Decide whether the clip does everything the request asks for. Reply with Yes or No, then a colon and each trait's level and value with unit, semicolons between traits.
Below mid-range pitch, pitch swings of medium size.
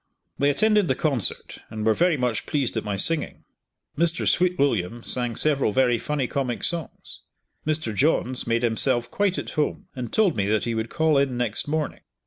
Yes: low, 130 Hz; average, 5.0 semitones